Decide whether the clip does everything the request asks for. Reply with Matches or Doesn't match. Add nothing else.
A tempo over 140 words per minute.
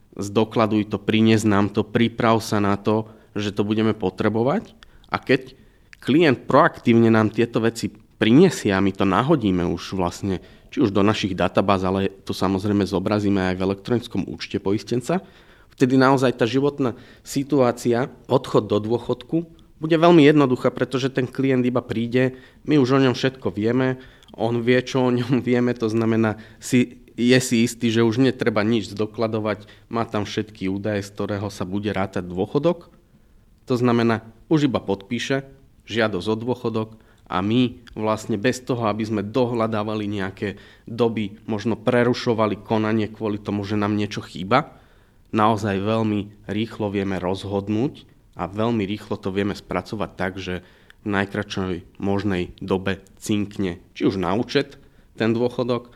Matches